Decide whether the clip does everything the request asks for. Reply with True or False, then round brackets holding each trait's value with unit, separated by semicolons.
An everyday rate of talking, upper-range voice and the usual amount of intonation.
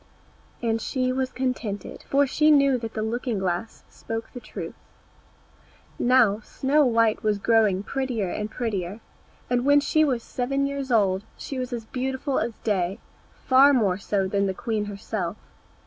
True (160 wpm; 230 Hz; 4.1 semitones)